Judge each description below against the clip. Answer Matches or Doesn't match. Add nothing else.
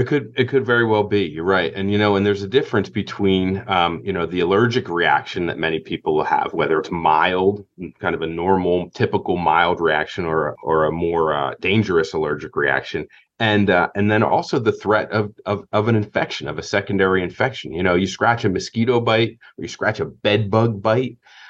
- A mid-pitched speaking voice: Doesn't match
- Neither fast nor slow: Doesn't match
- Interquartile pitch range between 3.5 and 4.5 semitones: Doesn't match